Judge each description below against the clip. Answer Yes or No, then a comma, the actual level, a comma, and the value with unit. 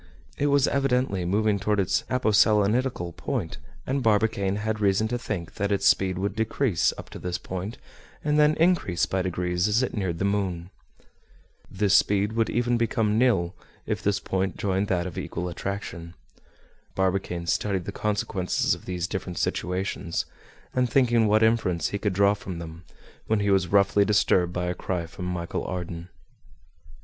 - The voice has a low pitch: Yes, low, 100 Hz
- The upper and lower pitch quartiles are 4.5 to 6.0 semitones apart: No, average, 3.4 semitones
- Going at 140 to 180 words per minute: Yes, average, 165 wpm